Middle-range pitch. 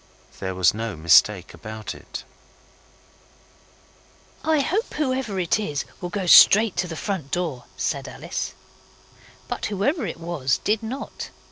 Yes: medium, 180 Hz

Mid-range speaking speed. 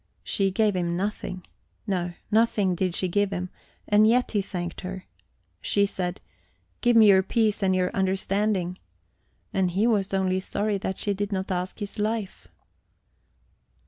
Yes: average, 155 wpm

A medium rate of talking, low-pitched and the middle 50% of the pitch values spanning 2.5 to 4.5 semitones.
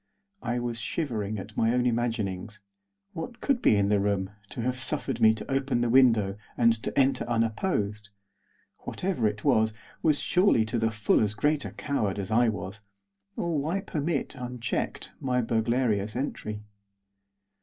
Yes: average, 160 wpm; low, 115 Hz; average, 3.9 semitones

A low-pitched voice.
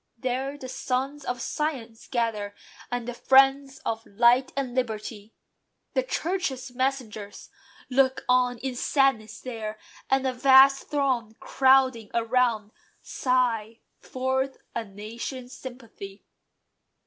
No: very high, 250 Hz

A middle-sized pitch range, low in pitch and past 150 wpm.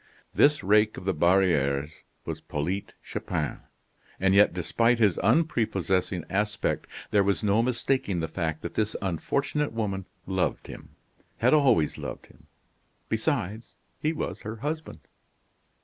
No: average, 4.4 semitones; low, 100 Hz; slow, 135 wpm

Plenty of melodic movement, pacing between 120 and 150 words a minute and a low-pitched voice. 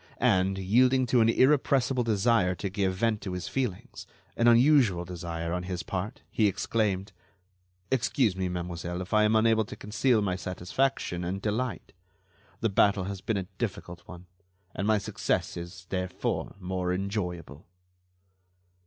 No: average, 4.0 semitones; average, 145 wpm; low, 100 Hz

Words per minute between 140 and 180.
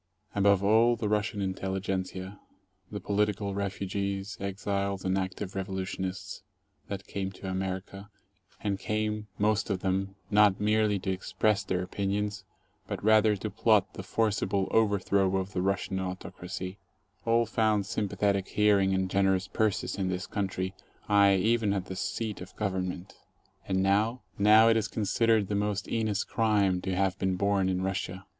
Yes: average, 155 wpm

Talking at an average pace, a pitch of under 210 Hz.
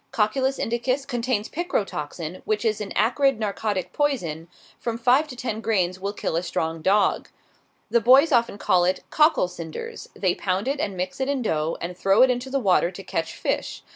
No: average, 190 wpm; high, 215 Hz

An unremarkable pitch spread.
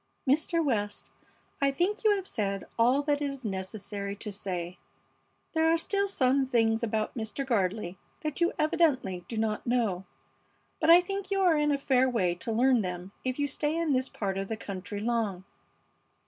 No: wide, 6.5 semitones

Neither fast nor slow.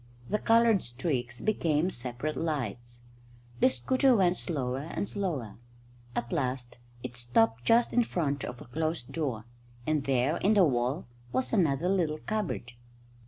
Yes: average, 145 wpm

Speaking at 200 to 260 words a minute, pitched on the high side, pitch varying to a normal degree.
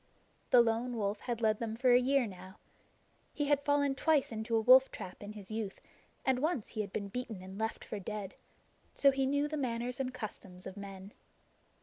Yes: fast, 205 wpm; high, 230 Hz; average, 4.4 semitones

